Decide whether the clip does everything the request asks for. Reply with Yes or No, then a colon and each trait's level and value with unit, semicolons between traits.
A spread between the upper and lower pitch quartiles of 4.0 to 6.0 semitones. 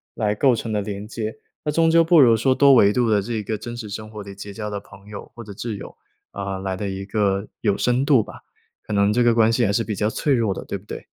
No: average, 2.9 semitones